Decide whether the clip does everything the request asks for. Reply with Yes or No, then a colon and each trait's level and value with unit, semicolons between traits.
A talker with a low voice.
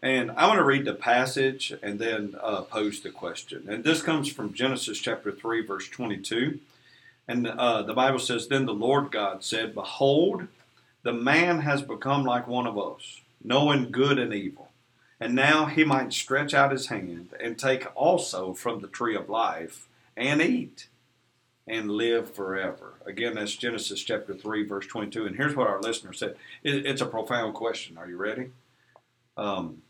Yes: low, 120 Hz